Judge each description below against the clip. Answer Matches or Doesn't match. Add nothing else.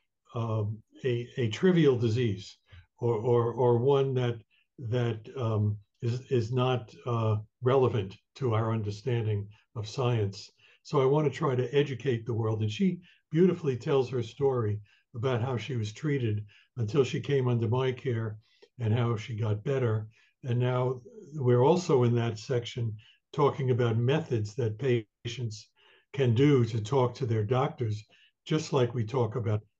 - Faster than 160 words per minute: Doesn't match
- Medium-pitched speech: Doesn't match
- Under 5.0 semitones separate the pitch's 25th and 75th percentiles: Matches